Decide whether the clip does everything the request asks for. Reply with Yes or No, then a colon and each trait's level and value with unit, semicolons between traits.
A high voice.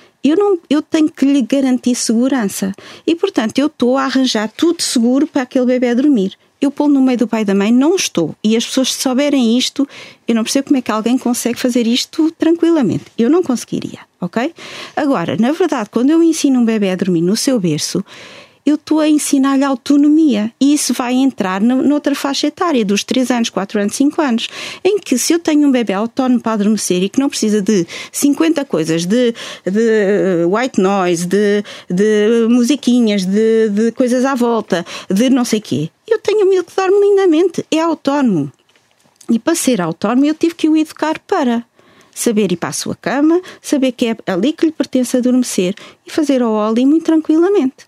Yes: very high, 255 Hz